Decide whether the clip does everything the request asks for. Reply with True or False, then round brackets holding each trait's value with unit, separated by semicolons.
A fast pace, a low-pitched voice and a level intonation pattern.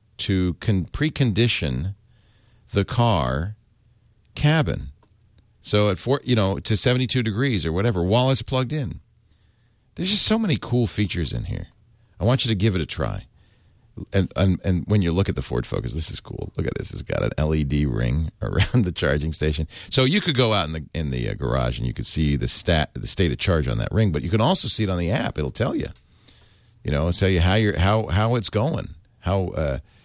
False (220 wpm; 105 Hz; 5.0 semitones)